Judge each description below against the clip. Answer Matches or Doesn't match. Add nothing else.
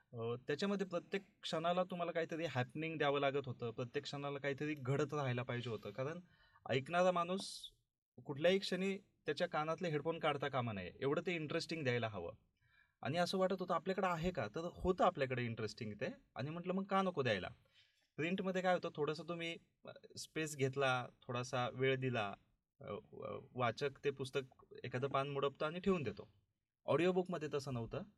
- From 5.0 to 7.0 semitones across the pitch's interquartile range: Matches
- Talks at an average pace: Doesn't match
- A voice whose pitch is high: Doesn't match